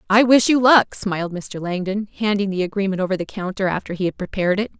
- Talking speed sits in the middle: No, fast, 225 wpm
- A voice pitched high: Yes, high, 200 Hz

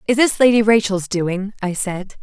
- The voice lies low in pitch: No, high, 205 Hz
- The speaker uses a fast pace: No, average, 190 wpm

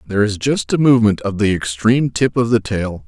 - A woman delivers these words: No, male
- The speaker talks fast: Yes, fast, 235 wpm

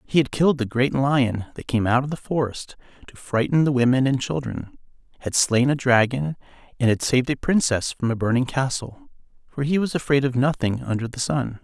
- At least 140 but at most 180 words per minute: No, fast, 205 wpm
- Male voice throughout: Yes, male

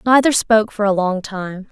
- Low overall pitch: No, high, 210 Hz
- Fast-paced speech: Yes, fast, 210 wpm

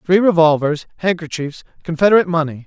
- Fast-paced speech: No, slow, 110 wpm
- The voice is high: No, medium, 165 Hz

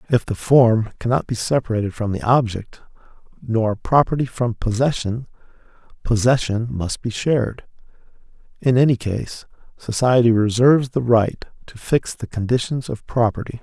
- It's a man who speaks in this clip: Yes, male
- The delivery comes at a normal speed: No, slow, 130 wpm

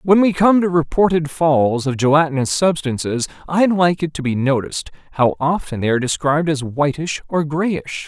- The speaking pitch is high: No, medium, 155 Hz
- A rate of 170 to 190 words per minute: Yes, average, 180 wpm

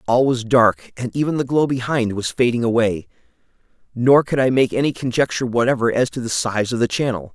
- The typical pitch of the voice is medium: No, low, 125 Hz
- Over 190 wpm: Yes, fast, 205 wpm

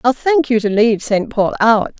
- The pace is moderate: No, fast, 240 wpm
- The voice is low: No, high, 225 Hz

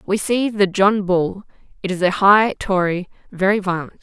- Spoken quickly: No, average, 180 wpm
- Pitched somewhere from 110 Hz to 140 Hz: No, high, 195 Hz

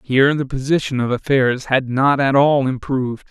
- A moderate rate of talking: Yes, average, 180 wpm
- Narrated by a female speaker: No, male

